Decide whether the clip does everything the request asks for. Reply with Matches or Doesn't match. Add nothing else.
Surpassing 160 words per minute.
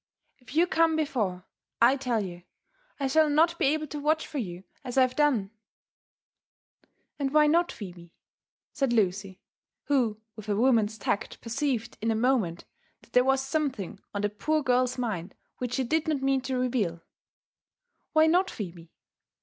Matches